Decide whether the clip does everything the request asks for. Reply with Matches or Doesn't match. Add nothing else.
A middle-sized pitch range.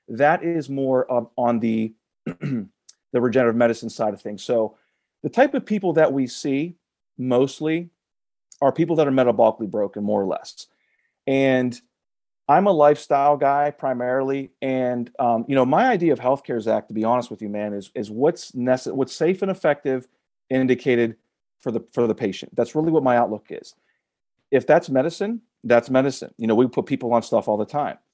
Matches